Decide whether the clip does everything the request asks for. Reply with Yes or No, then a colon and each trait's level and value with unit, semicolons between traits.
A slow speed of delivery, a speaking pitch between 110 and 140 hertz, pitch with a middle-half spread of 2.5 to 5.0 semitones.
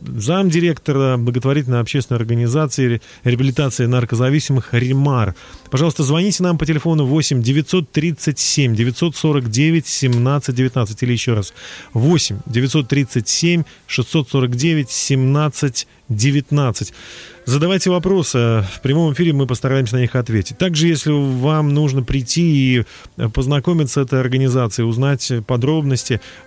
Yes: slow, 90 wpm; low, 135 Hz; average, 3.8 semitones